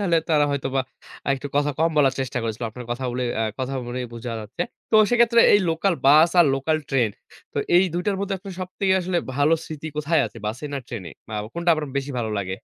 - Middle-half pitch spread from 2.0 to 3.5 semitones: No, wide, 5.5 semitones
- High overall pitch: No, medium, 145 Hz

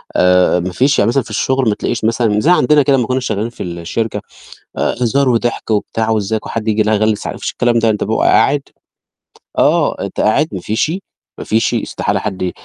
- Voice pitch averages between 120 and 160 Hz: No, low, 110 Hz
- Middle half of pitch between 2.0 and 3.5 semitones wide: Yes, average, 2.9 semitones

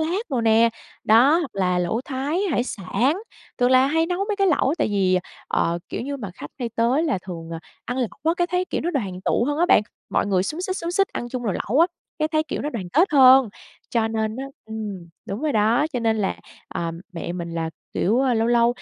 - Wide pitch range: Yes, wide, 6.5 semitones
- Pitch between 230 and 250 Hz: Yes, high, 240 Hz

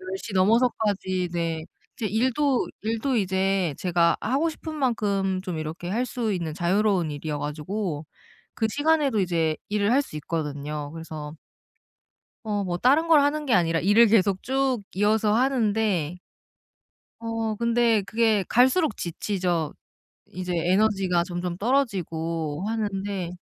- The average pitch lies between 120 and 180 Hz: No, high, 200 Hz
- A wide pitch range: No, average, 5.0 semitones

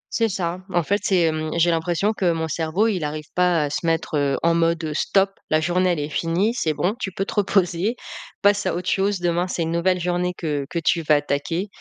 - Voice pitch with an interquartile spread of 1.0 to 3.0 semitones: Yes, average, 2.7 semitones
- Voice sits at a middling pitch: Yes, medium, 170 Hz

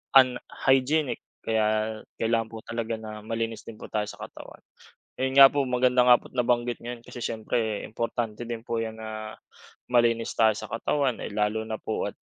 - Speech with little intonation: Yes, narrow, 2.0 semitones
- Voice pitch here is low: Yes, low, 115 Hz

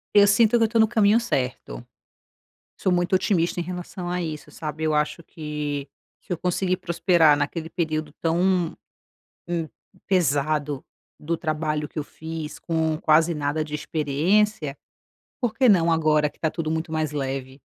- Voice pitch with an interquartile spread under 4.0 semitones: Yes, average, 3.0 semitones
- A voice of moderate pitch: Yes, medium, 160 Hz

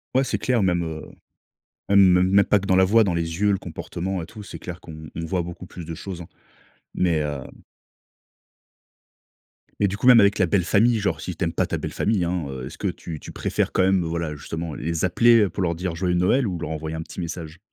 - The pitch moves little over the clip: No, average, 3.2 semitones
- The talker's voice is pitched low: Yes, very low, 90 Hz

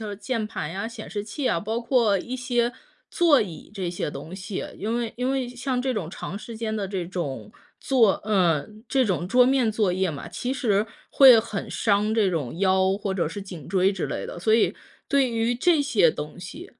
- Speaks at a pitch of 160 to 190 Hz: No, high, 215 Hz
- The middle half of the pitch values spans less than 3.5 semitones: No, average, 4.5 semitones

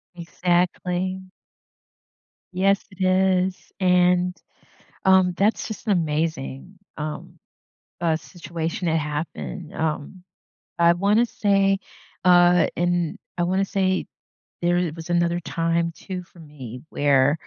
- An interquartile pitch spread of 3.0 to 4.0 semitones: No, narrow, 2.5 semitones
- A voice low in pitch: No, medium, 175 Hz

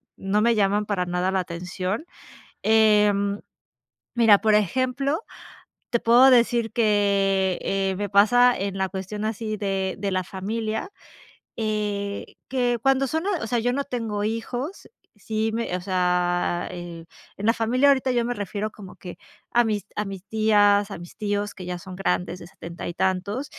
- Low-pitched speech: No, high, 205 Hz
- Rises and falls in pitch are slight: No, average, 3.2 semitones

